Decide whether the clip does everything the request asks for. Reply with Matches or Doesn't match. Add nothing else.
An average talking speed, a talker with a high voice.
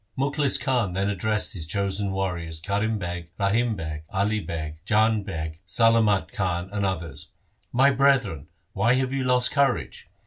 Doesn't match